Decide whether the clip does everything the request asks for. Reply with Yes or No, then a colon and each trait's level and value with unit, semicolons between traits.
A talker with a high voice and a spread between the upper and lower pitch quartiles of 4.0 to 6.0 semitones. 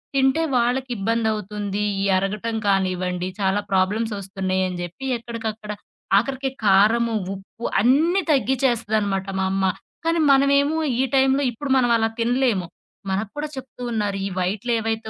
Yes: high, 225 Hz; average, 4.9 semitones